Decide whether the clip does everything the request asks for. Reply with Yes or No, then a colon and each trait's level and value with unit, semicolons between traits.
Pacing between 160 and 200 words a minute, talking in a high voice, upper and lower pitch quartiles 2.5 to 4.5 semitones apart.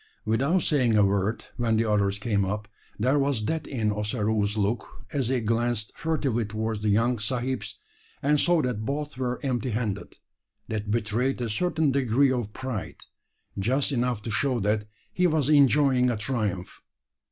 No: average, 165 wpm; low, 120 Hz; average, 4.0 semitones